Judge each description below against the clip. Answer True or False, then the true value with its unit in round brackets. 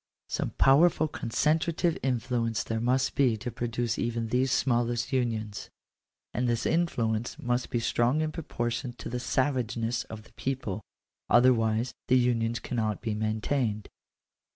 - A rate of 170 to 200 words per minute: False (145 wpm)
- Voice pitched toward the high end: False (120 Hz)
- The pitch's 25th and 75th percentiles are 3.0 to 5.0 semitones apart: False (2.4 semitones)